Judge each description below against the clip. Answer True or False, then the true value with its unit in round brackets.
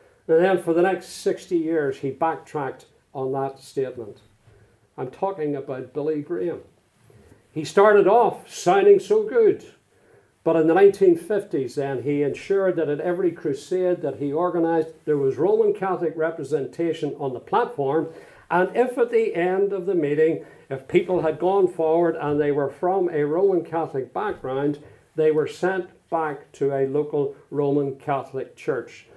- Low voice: False (160 Hz)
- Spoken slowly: False (155 wpm)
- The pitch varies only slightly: False (4.8 semitones)